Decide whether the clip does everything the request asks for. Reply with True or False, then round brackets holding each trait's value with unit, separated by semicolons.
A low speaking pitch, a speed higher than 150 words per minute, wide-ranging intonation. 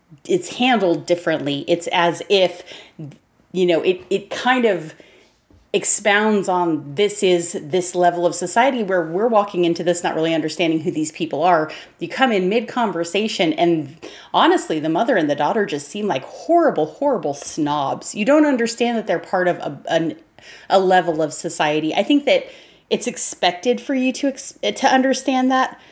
False (185 Hz; 170 wpm; 5.9 semitones)